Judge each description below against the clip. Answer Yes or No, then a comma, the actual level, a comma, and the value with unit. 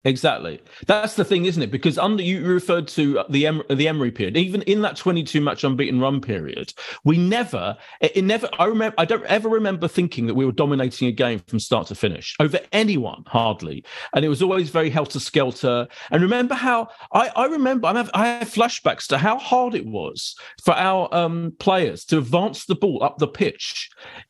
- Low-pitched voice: No, medium, 170 Hz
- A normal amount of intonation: No, wide, 6.8 semitones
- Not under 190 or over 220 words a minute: Yes, fast, 205 wpm